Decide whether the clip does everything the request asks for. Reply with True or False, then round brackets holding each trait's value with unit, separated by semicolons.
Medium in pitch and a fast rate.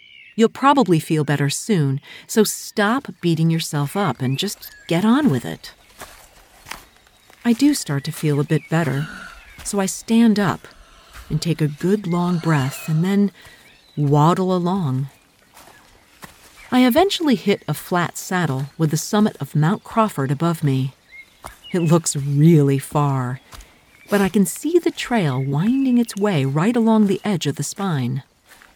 False (170 Hz; 150 wpm)